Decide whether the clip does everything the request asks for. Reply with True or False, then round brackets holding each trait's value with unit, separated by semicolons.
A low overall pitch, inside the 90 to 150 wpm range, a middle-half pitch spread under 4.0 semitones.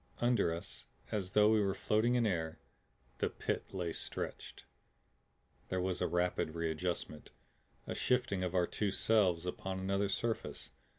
True (95 Hz; 145 wpm; 3.3 semitones)